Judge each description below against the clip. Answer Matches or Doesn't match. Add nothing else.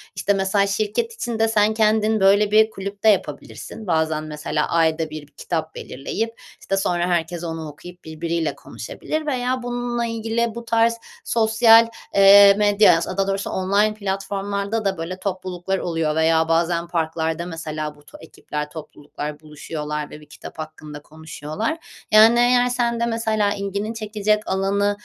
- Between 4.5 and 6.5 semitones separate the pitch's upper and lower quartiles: Matches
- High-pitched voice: Matches